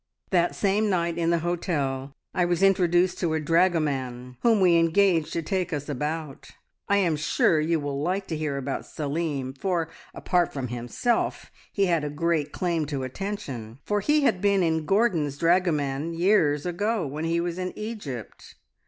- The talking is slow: No, average, 170 wpm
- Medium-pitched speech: Yes, medium, 165 Hz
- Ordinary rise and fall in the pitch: Yes, average, 4.0 semitones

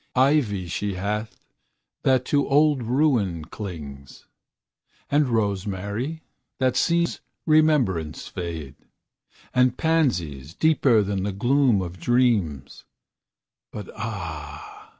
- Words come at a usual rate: No, slow, 95 wpm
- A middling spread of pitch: No, wide, 7.0 semitones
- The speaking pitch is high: No, low, 105 Hz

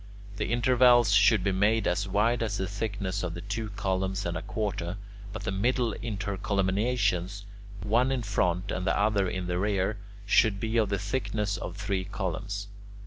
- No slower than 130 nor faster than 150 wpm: No, average, 170 wpm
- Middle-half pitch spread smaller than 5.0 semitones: Yes, narrow, 2.5 semitones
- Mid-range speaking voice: No, low, 100 Hz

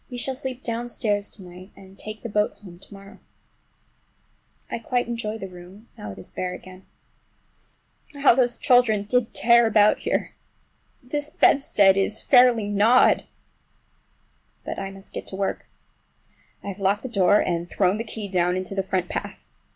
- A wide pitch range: No, average, 3.8 semitones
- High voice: Yes, high, 205 Hz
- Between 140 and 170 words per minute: Yes, average, 165 wpm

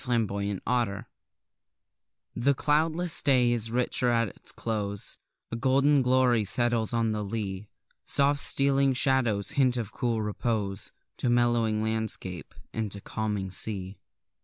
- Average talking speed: No, slow, 125 wpm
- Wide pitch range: No, average, 3.3 semitones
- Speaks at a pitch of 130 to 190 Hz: No, low, 115 Hz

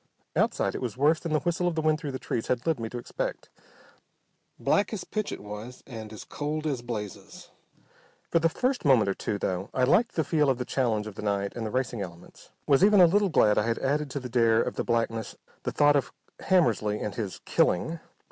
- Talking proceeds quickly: Yes, fast, 230 wpm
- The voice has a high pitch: No, low, 125 Hz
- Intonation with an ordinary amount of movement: No, wide, 6.2 semitones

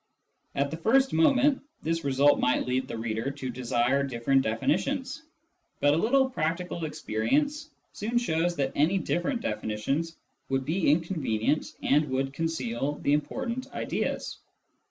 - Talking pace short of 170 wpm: Yes, slow, 135 wpm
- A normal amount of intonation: No, wide, 6.3 semitones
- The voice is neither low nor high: Yes, medium, 150 Hz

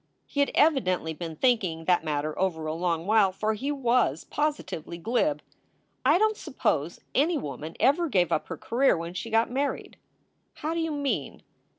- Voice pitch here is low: No, high, 220 Hz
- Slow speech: No, average, 180 wpm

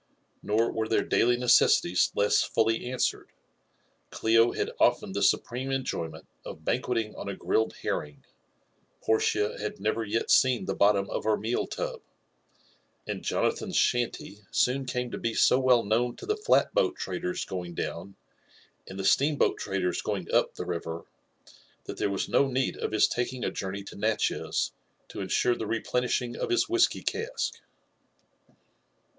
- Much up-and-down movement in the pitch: No, average, 4.1 semitones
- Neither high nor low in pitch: No, low, 115 Hz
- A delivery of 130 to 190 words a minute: Yes, average, 160 wpm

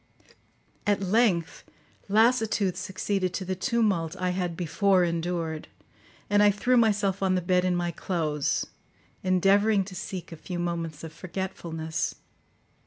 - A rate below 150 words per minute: Yes, slow, 135 wpm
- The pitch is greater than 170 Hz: Yes, medium, 185 Hz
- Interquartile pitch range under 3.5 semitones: Yes, average, 2.9 semitones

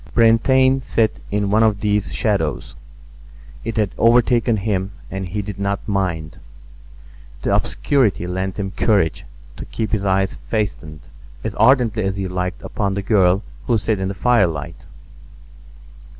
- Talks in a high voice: No, low, 100 Hz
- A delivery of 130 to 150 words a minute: Yes, average, 145 wpm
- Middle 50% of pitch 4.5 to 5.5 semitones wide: No, average, 2.8 semitones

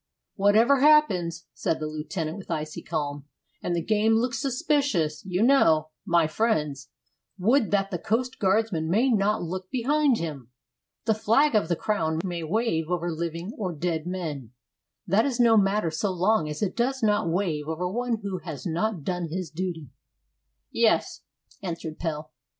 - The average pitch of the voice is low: No, medium, 185 Hz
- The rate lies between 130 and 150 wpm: No, average, 160 wpm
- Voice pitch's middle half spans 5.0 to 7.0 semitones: Yes, wide, 5.5 semitones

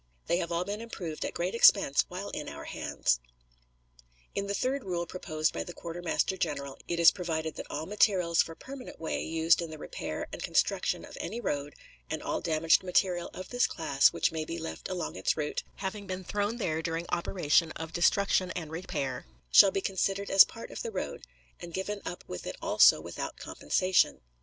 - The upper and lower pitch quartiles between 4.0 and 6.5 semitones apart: No, average, 3.3 semitones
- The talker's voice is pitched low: No, medium, 175 Hz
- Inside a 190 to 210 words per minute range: Yes, average, 195 wpm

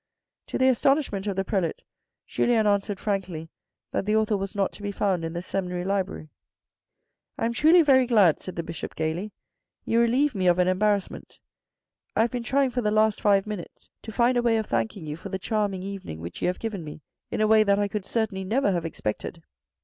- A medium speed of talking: No, fast, 220 wpm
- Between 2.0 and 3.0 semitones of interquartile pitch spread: No, average, 3.6 semitones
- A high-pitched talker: Yes, high, 200 Hz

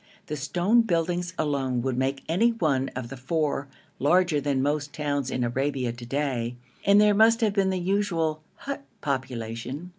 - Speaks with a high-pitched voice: No, medium, 145 Hz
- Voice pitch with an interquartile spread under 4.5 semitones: No, average, 5.3 semitones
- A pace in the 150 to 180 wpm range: Yes, average, 170 wpm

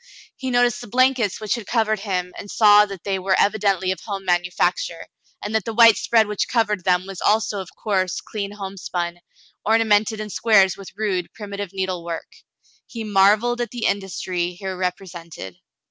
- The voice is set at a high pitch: Yes, high, 200 Hz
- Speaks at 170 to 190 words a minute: Yes, average, 175 wpm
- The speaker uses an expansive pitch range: No, average, 2.7 semitones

